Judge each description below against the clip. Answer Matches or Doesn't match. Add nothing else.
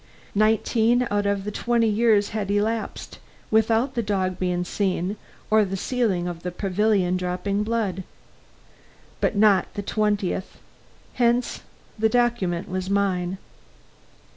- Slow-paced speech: Matches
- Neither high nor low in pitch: Doesn't match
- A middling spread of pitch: Matches